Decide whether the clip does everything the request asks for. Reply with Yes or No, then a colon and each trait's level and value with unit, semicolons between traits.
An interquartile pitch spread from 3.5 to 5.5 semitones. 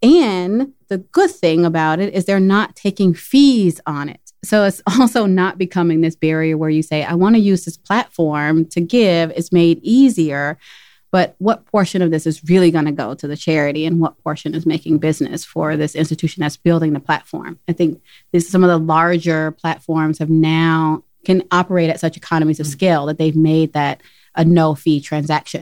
No: average, 2.9 semitones